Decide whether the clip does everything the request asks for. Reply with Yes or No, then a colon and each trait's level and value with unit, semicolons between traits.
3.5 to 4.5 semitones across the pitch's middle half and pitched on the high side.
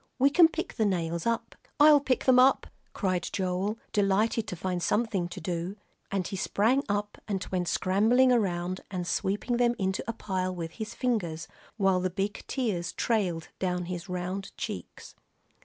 Yes: average, 4.1 semitones; high, 195 Hz